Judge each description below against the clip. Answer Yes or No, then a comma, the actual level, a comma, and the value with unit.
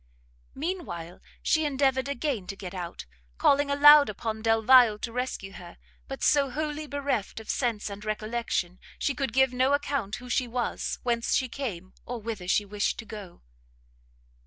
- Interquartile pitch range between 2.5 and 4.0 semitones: No, average, 5.0 semitones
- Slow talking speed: No, average, 165 wpm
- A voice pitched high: Yes, high, 240 Hz